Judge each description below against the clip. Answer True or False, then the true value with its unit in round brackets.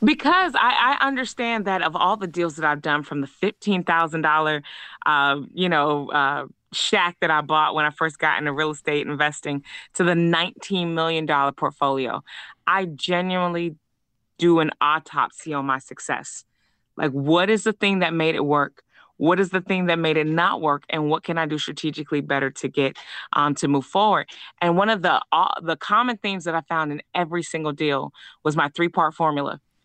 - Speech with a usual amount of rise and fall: True (3.3 semitones)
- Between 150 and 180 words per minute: False (190 wpm)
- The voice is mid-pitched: True (160 Hz)